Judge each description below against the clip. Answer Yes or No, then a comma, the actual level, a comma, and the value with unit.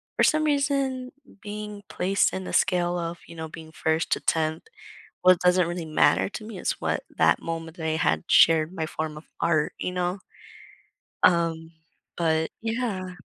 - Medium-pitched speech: Yes, medium, 175 Hz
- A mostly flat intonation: No, average, 3.6 semitones